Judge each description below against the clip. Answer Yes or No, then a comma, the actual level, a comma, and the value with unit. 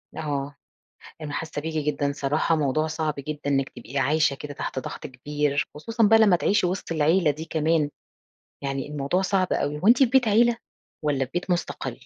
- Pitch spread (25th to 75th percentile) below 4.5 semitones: Yes, average, 3.7 semitones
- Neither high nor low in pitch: Yes, medium, 150 Hz